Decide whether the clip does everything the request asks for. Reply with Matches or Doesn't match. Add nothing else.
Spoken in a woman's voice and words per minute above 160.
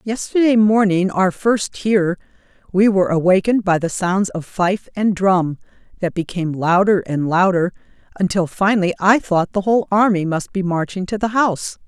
Doesn't match